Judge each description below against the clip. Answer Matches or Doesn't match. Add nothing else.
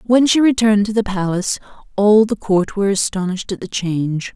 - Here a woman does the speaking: Matches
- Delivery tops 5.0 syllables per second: Matches